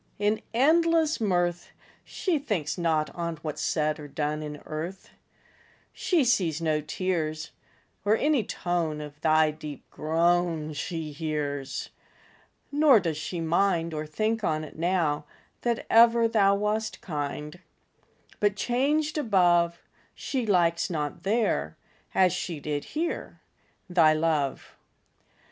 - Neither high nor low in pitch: Yes, medium, 170 Hz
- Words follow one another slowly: Yes, slow, 120 wpm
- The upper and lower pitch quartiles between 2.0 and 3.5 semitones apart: No, wide, 5.5 semitones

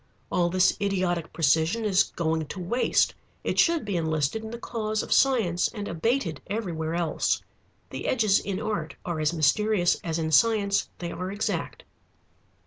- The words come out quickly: No, average, 160 wpm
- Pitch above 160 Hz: Yes, medium, 185 Hz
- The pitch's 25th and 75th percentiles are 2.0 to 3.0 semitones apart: No, average, 4.7 semitones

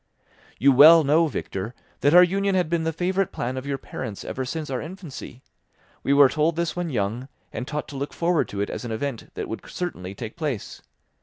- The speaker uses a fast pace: Yes, fast, 215 wpm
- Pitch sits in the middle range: Yes, medium, 145 Hz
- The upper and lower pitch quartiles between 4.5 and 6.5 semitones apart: Yes, average, 5.0 semitones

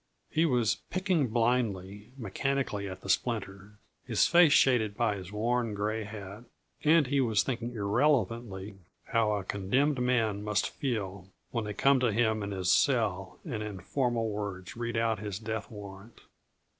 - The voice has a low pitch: Yes, low, 110 Hz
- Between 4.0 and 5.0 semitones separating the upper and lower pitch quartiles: No, average, 3.5 semitones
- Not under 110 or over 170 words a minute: Yes, average, 155 wpm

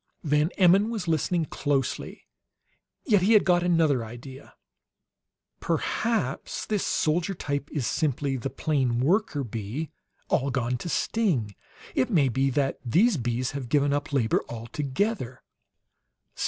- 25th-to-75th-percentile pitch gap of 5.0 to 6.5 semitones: Yes, average, 5.3 semitones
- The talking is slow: Yes, slow, 130 wpm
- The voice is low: No, medium, 145 Hz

